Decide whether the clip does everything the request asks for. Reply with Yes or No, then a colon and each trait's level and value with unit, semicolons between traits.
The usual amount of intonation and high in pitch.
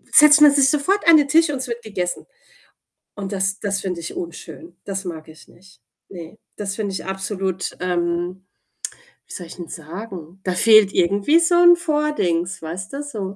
No: wide, 8.0 semitones; high, 195 Hz